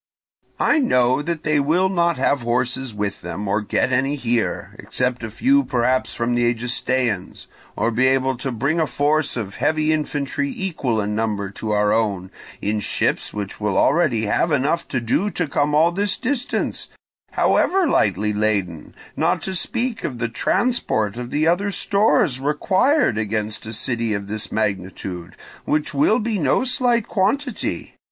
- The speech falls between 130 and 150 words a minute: No, average, 165 wpm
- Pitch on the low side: Yes, low, 130 Hz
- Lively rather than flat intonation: Yes, wide, 7.6 semitones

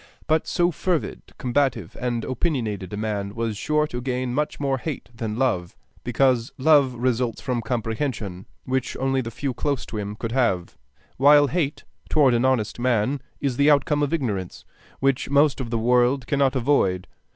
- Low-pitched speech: Yes, low, 125 Hz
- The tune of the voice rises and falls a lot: No, average, 3.6 semitones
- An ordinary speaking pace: Yes, average, 170 wpm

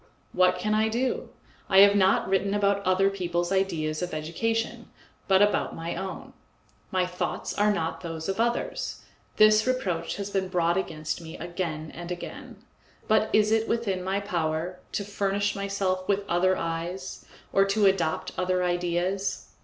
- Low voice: No, high, 190 Hz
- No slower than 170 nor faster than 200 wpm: No, average, 160 wpm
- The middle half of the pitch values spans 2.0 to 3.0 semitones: Yes, narrow, 2.6 semitones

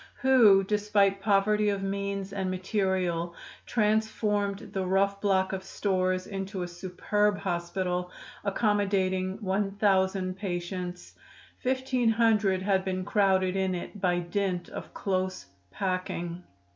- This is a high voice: Yes, high, 195 Hz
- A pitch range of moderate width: No, narrow, 1.7 semitones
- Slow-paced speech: Yes, slow, 115 wpm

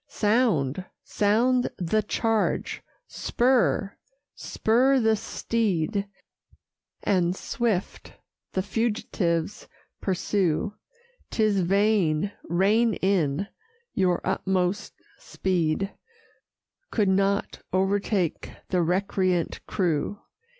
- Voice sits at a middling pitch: No, high, 195 Hz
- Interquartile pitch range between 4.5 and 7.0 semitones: No, average, 3.3 semitones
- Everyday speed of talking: No, slow, 75 wpm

